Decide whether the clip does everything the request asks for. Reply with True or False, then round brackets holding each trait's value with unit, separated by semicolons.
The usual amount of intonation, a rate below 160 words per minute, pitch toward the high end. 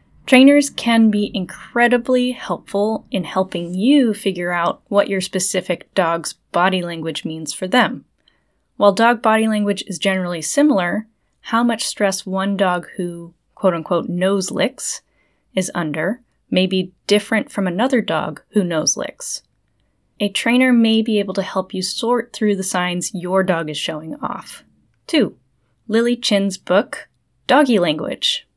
True (4.0 semitones; 145 wpm; 195 Hz)